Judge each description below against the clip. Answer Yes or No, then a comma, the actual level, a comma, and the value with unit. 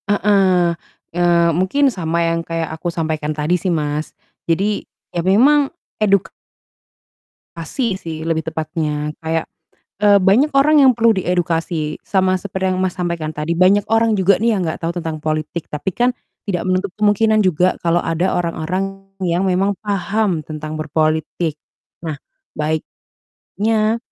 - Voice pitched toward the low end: No, medium, 175 Hz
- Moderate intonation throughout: Yes, average, 3.8 semitones